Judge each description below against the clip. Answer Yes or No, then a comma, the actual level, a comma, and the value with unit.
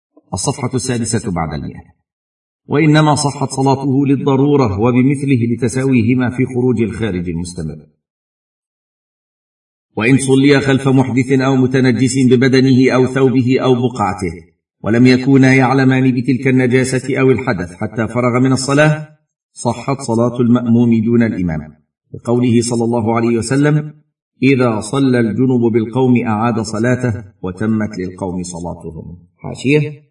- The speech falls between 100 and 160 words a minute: Yes, average, 110 wpm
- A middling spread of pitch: Yes, average, 3.4 semitones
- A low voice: Yes, low, 125 Hz